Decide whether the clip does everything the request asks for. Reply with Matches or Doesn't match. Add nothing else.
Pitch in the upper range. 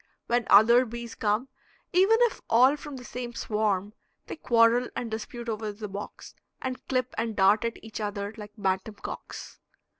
Matches